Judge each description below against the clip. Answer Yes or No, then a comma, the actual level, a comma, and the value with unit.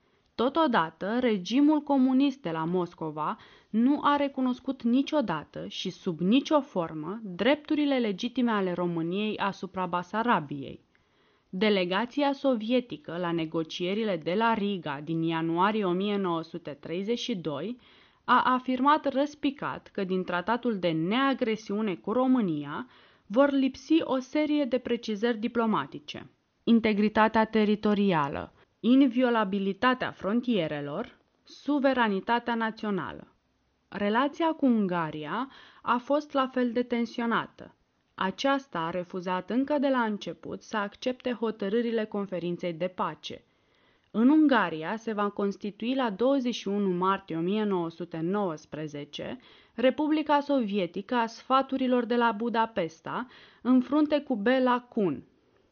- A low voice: No, high, 225 Hz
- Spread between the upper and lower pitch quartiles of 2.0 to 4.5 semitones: No, wide, 5.6 semitones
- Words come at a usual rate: No, slow, 105 wpm